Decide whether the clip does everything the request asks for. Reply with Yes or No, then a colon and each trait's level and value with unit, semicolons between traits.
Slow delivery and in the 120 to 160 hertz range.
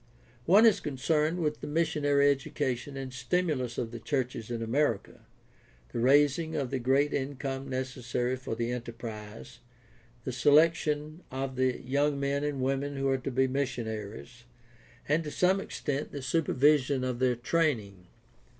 No: average, 150 wpm; low, 135 Hz